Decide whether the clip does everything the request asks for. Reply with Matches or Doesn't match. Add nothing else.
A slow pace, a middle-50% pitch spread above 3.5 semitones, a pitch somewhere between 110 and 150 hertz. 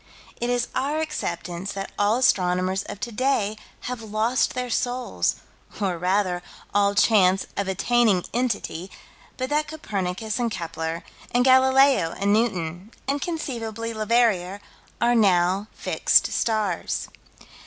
Doesn't match